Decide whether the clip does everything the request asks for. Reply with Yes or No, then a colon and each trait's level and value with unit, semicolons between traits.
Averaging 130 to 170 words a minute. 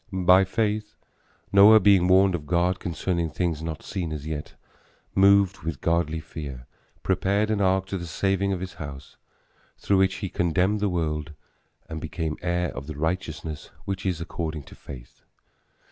Yes: average, 160 wpm